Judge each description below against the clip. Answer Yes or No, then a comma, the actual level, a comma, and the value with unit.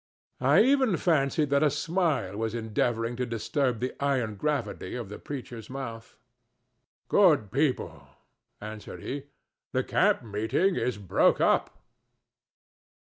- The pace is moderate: No, slow, 125 wpm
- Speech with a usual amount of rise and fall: Yes, average, 4.9 semitones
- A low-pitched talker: Yes, low, 125 Hz